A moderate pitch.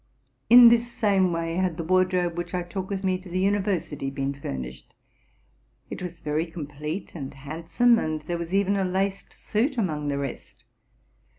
Yes: medium, 175 Hz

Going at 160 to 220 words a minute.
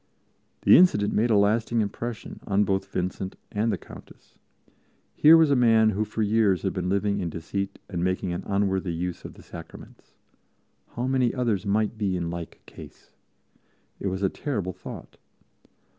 Yes: average, 170 wpm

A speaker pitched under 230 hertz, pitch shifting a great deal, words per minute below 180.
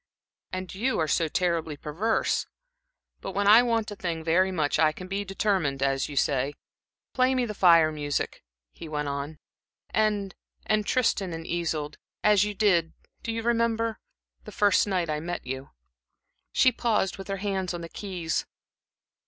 No: medium, 185 Hz; average, 4.9 semitones; average, 170 wpm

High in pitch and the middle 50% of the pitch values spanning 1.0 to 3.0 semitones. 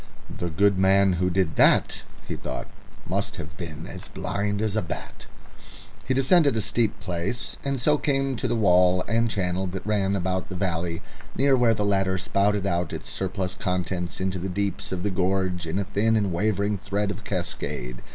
No: very low, 95 Hz; narrow, 2.6 semitones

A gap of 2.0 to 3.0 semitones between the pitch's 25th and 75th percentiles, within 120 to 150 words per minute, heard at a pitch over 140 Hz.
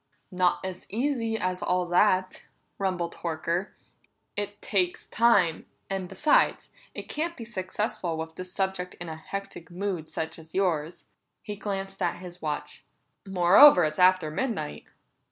Yes: average, 2.7 semitones; average, 140 wpm; medium, 185 Hz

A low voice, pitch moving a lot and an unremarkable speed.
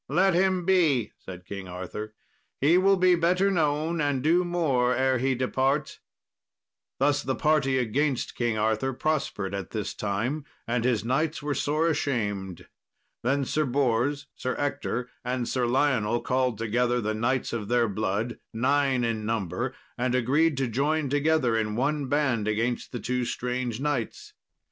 No: low, 130 Hz; average, 4.3 semitones; average, 155 wpm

